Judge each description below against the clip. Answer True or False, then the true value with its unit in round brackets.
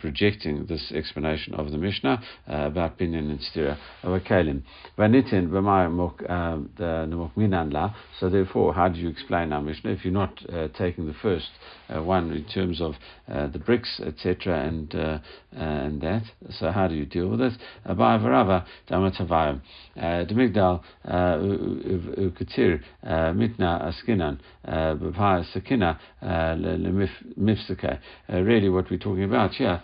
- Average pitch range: True (3.3 semitones)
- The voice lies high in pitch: False (90 Hz)